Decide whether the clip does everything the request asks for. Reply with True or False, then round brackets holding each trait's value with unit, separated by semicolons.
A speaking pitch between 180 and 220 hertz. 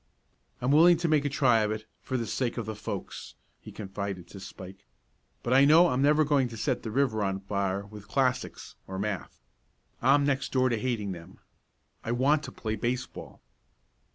False (120 Hz)